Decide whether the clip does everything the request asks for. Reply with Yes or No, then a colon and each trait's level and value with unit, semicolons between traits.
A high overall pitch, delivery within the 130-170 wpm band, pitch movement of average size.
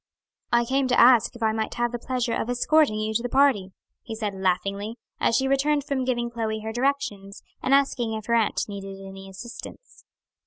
No: high, 235 Hz; average, 200 wpm; average, 3.5 semitones